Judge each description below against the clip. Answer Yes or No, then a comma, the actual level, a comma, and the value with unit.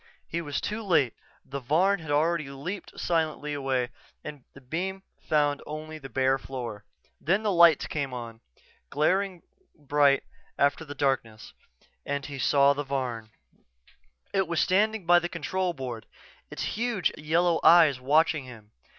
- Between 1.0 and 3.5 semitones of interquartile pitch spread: No, average, 4.2 semitones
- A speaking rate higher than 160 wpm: No, average, 150 wpm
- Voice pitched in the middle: Yes, medium, 150 Hz